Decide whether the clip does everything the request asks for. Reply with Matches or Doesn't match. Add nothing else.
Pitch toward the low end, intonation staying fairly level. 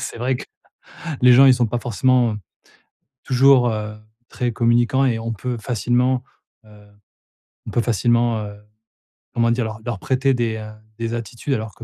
Matches